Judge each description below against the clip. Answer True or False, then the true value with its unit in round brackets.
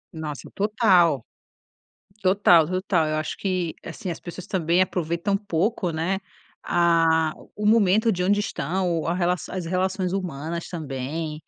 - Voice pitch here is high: False (175 Hz)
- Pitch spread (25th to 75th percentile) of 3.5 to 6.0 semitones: False (2.8 semitones)